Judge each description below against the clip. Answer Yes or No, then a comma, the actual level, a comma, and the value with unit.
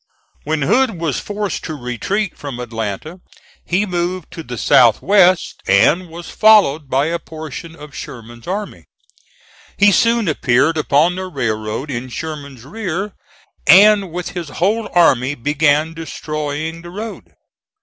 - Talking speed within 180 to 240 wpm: No, average, 140 wpm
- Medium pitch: Yes, medium, 160 Hz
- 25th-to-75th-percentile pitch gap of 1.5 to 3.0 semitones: No, average, 5.0 semitones